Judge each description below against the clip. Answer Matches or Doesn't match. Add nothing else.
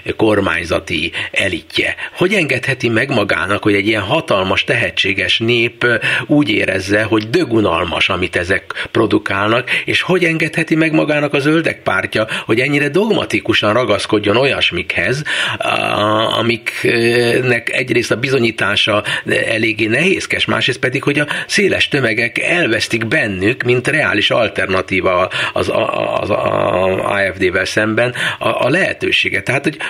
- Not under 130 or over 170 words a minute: Doesn't match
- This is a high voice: Doesn't match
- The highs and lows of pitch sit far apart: Matches